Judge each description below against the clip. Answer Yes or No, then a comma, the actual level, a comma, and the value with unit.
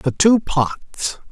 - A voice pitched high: No, medium, 170 Hz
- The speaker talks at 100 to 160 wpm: Yes, slow, 135 wpm